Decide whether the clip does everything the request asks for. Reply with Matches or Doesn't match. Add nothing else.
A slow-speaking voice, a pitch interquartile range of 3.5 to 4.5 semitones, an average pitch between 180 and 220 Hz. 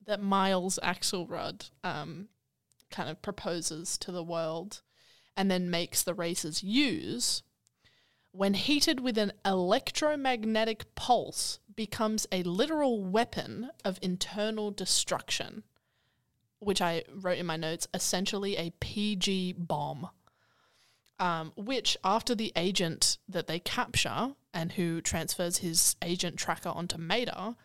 Matches